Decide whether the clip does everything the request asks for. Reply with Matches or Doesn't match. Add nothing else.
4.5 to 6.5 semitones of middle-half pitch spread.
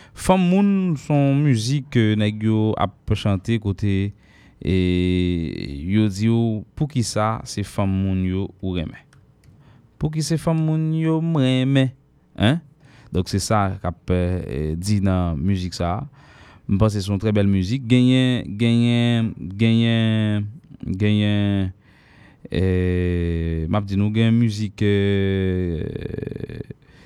Matches